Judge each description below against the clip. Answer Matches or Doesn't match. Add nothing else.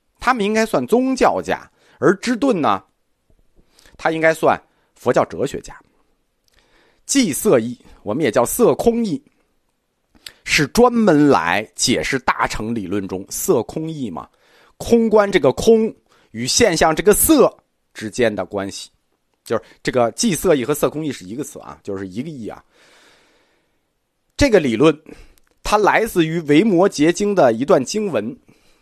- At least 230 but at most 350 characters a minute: Doesn't match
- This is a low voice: Doesn't match